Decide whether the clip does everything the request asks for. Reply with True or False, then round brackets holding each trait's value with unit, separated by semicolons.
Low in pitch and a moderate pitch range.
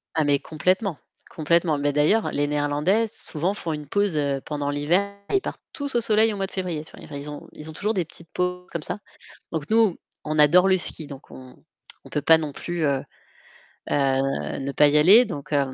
False (155 Hz; 4.5 semitones)